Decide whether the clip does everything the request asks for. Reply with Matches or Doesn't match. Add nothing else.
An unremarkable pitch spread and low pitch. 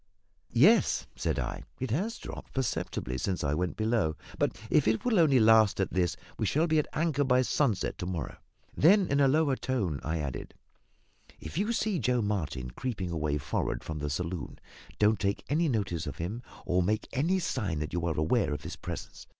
Doesn't match